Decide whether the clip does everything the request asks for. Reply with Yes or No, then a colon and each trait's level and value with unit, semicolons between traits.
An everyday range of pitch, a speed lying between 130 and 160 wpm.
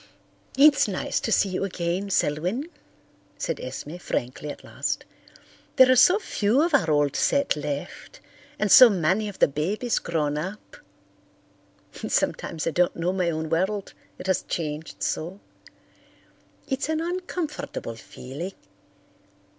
No: wide, 8.4 semitones; slow, 135 wpm